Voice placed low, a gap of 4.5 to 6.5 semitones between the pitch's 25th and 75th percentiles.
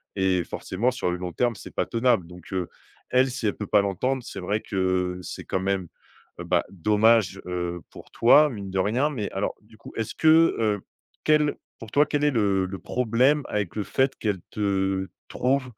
Yes: low, 105 Hz; average, 5.0 semitones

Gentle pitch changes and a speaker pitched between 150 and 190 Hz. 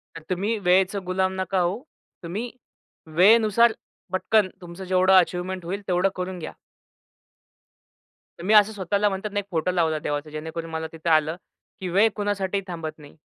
No: average, 3.0 semitones; medium, 185 Hz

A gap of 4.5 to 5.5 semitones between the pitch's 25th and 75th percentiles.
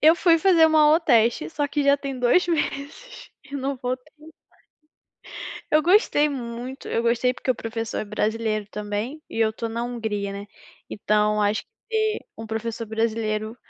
Yes: average, 5.0 semitones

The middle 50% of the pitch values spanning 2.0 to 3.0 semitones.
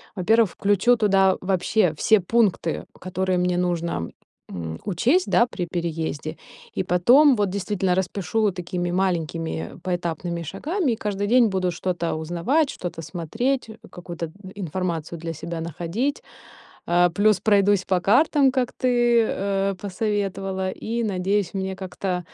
No: average, 3.5 semitones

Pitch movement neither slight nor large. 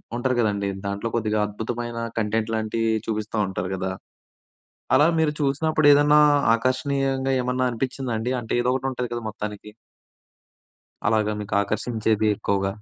Yes: average, 3.4 semitones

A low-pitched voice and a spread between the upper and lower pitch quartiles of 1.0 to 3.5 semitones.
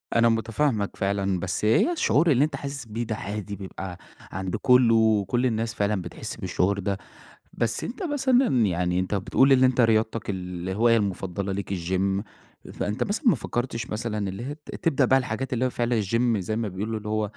No: low, 110 Hz; average, 4.2 semitones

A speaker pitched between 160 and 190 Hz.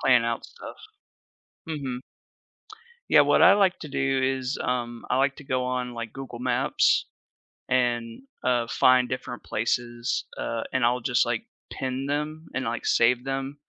No: low, 125 Hz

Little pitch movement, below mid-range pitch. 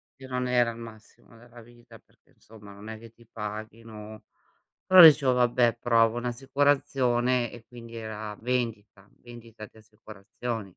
Yes: narrow, 2.0 semitones; low, 115 Hz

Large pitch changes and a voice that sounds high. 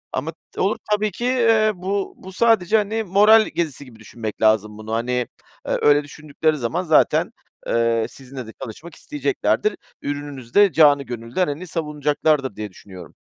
No: wide, 8.7 semitones; medium, 150 Hz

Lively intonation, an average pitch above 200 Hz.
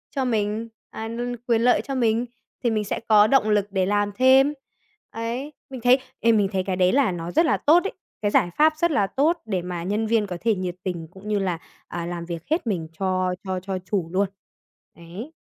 No: average, 4.8 semitones; high, 210 Hz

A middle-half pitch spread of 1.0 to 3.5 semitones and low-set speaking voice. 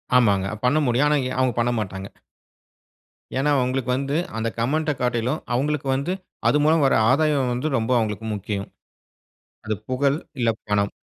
No: average, 4.0 semitones; low, 125 Hz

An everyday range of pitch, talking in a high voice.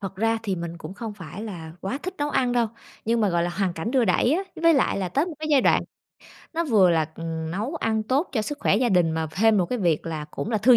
No: wide, 6.4 semitones; high, 210 Hz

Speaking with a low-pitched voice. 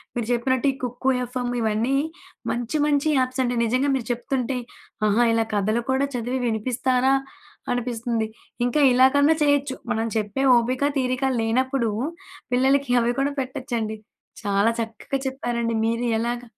No: high, 245 Hz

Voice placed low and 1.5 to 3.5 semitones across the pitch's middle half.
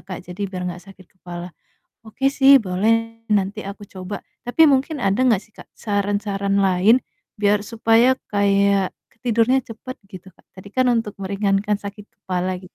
No: high, 200 Hz; average, 2.9 semitones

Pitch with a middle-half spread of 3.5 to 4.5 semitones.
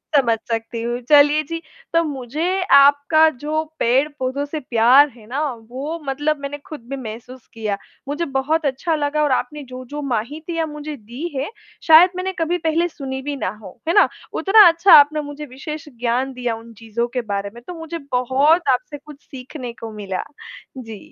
Yes: average, 3.9 semitones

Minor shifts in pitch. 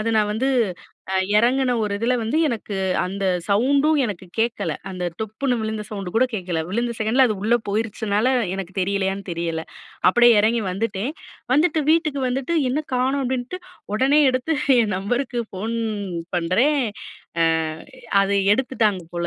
No: average, 4.5 semitones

